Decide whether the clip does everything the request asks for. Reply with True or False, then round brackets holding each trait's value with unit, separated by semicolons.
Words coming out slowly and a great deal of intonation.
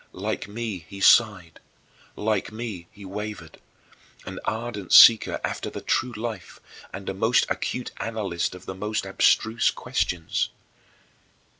False (130 wpm; 2.9 semitones)